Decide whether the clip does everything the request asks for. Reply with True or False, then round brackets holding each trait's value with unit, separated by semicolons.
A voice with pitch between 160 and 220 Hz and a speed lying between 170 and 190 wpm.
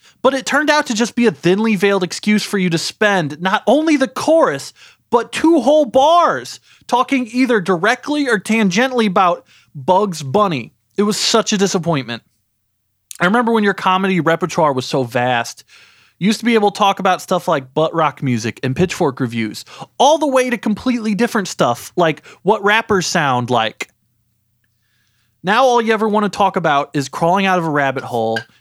True (190 Hz; 185 wpm)